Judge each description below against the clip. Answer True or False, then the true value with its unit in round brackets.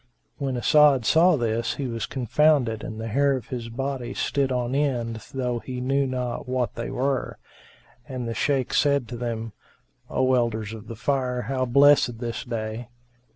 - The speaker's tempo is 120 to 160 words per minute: False (180 wpm)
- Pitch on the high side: False (125 Hz)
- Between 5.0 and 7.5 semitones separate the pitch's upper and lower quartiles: False (2.8 semitones)